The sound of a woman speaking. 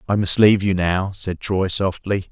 No: male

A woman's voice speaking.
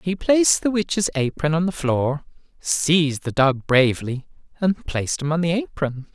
No: male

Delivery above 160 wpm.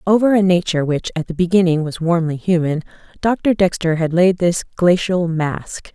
Yes: average, 170 wpm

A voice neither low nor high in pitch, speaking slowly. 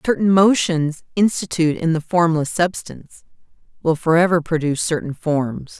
Yes: medium, 165 Hz; slow, 125 wpm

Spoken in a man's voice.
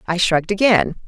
No: female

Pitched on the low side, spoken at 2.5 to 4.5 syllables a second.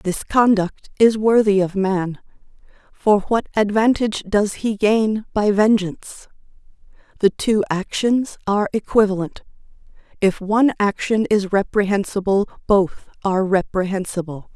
No: high, 205 Hz; 4.4 syllables/s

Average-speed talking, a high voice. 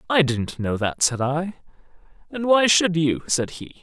No: average, 190 wpm; medium, 155 Hz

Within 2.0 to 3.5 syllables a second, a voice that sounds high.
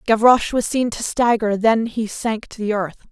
No: 4.9 syllables/s; high, 220 Hz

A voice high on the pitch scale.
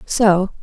Yes: high, 195 Hz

